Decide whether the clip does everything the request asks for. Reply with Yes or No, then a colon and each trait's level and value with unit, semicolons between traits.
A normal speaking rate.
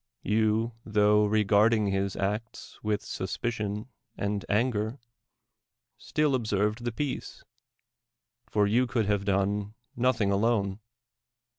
No: slow, 105 wpm